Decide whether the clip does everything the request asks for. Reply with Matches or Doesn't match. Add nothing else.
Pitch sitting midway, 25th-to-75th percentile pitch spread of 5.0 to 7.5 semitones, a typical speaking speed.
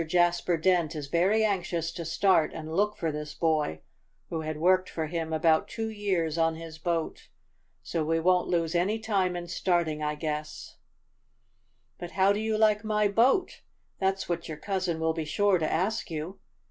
Doesn't match